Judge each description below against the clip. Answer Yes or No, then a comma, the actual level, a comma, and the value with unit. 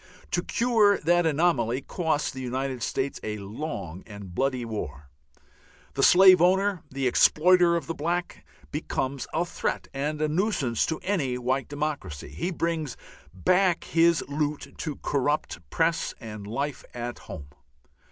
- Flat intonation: No, wide, 5.5 semitones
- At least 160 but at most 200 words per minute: No, average, 140 wpm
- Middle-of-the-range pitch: Yes, medium, 145 Hz